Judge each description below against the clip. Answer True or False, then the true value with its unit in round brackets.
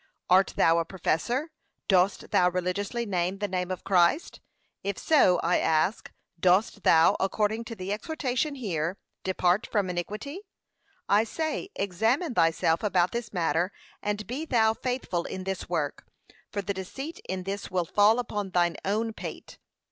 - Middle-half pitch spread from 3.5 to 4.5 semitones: True (3.9 semitones)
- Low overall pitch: False (195 Hz)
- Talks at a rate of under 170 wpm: True (155 wpm)